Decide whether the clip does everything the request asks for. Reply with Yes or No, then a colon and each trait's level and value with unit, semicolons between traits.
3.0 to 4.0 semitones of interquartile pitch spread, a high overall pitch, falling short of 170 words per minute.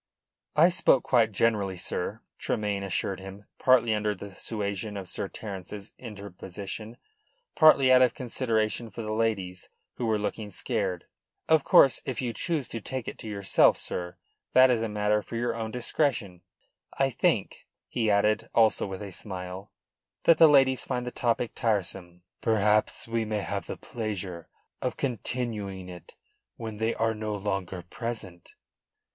No: average, 3.3 semitones; low, 110 Hz; average, 155 wpm